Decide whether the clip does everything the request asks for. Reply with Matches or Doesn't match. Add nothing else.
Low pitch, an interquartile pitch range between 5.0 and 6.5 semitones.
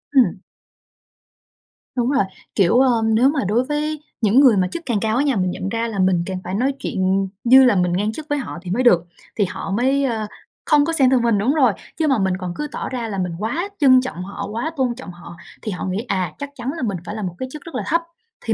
Doesn't match